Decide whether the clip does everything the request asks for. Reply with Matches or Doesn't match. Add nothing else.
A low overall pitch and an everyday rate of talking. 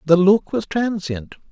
Doesn't match